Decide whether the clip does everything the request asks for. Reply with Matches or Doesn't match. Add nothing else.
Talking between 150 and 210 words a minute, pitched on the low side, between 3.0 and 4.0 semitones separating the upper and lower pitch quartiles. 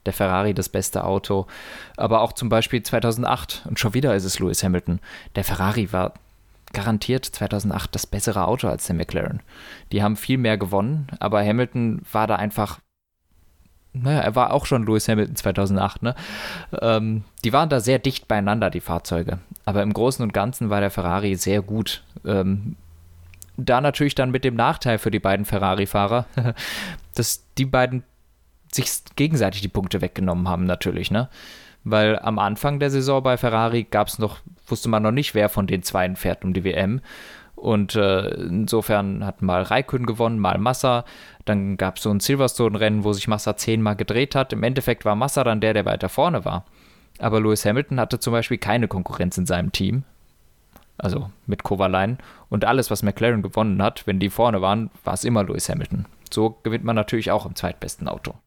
Matches